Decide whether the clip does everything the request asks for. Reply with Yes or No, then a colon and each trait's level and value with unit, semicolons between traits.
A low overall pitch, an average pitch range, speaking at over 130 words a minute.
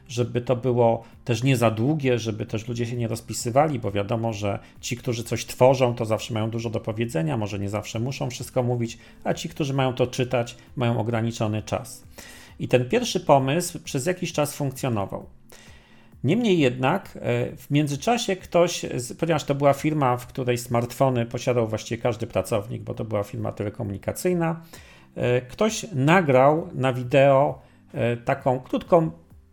Yes: low, 125 Hz; average, 3.7 semitones; average, 155 wpm